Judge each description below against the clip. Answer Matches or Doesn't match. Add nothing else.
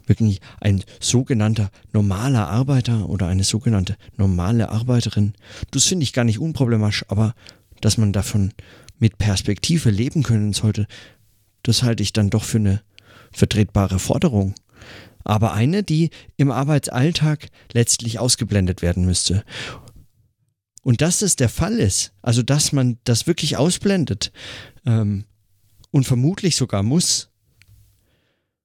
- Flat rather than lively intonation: Doesn't match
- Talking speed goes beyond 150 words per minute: Doesn't match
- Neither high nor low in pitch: Doesn't match